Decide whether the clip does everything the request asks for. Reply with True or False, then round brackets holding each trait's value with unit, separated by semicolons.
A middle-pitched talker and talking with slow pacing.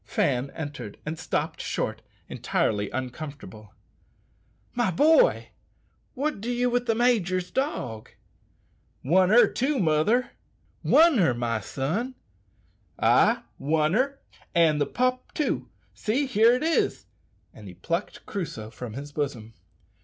True (175 Hz; 125 wpm)